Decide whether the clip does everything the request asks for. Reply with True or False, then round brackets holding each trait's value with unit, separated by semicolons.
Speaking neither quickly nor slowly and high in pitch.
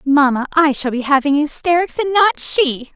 True (185 wpm; 300 Hz)